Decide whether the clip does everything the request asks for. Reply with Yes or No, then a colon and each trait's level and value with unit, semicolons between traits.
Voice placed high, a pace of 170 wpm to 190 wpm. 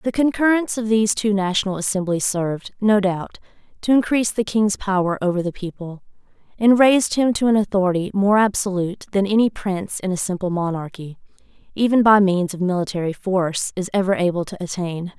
Yes: high, 195 Hz; average, 175 wpm